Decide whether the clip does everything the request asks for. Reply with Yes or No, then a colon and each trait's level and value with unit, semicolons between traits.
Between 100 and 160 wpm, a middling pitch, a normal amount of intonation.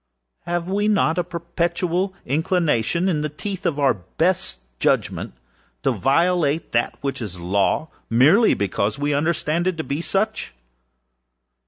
Yes: average, 140 wpm; medium, 165 Hz; average, 4.5 semitones